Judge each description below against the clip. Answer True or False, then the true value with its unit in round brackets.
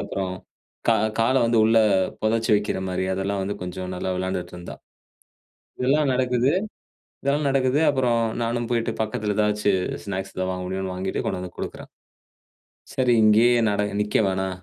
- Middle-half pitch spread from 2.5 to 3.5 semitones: False (4.1 semitones)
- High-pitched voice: False (105 Hz)